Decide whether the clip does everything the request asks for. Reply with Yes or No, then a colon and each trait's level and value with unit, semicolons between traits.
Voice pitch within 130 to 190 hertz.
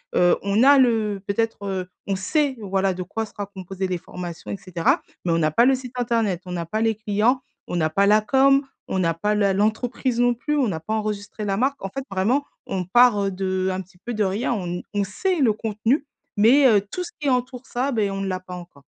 No: high, 205 Hz